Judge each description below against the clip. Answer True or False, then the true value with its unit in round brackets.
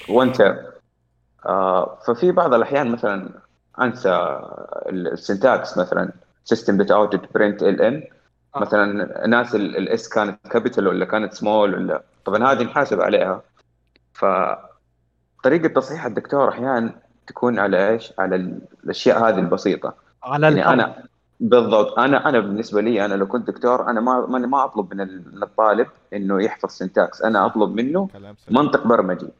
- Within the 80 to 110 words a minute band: False (130 wpm)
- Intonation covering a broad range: False (4.5 semitones)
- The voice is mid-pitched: False (105 Hz)